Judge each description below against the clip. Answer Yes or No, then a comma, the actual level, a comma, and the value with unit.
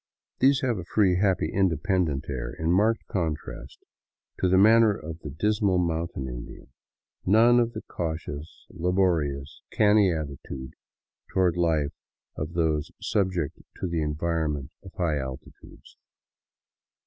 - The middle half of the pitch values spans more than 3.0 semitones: Yes, average, 4.4 semitones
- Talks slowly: Yes, slow, 125 wpm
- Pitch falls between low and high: No, very low, 85 Hz